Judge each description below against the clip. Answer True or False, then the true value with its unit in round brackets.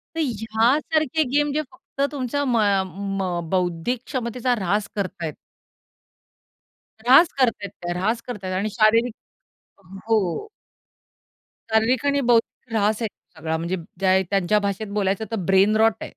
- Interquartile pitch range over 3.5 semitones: True (4.2 semitones)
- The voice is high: True (215 Hz)